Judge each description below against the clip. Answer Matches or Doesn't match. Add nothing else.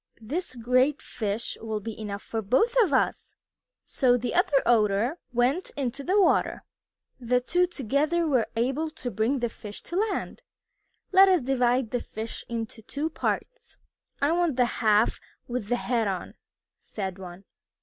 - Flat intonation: Doesn't match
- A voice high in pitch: Matches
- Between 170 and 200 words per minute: Doesn't match